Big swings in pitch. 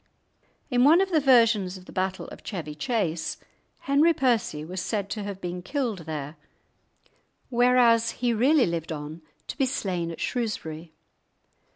Yes: wide, 6.6 semitones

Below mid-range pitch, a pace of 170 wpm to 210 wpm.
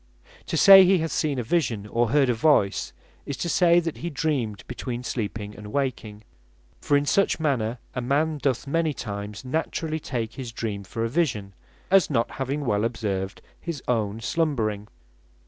Yes: low, 125 Hz; average, 180 wpm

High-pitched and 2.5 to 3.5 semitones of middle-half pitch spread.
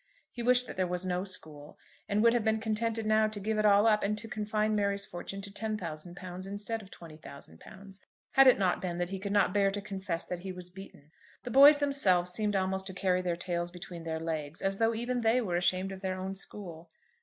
Yes: high, 195 Hz; average, 3.2 semitones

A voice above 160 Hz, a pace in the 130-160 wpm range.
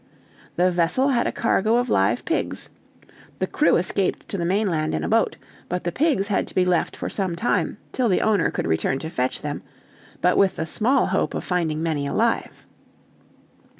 No: medium, 185 Hz; average, 195 wpm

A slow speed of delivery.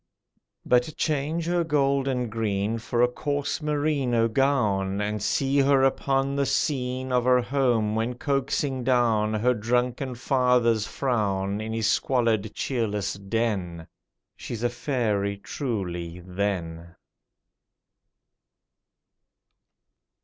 Yes: slow, 110 wpm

